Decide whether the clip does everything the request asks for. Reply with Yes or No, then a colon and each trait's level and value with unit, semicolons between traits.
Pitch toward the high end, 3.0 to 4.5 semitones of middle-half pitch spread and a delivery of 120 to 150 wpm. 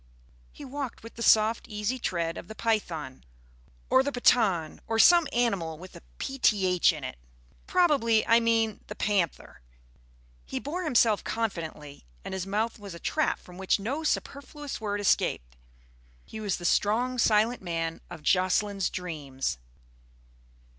No: high, 210 Hz; average, 5.1 semitones; average, 145 wpm